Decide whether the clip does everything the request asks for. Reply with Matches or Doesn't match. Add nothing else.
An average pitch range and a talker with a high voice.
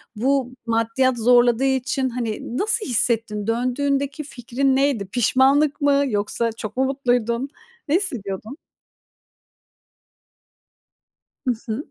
Matches